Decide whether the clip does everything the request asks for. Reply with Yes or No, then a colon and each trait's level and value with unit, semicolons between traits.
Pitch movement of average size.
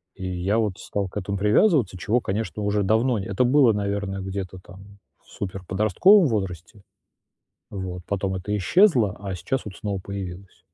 No: narrow, 2.2 semitones